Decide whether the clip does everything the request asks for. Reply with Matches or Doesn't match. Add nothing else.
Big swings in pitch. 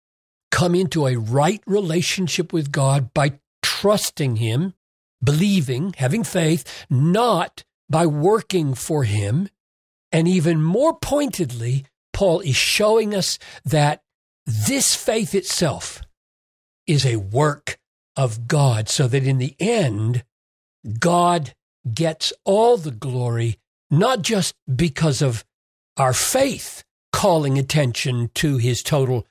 Matches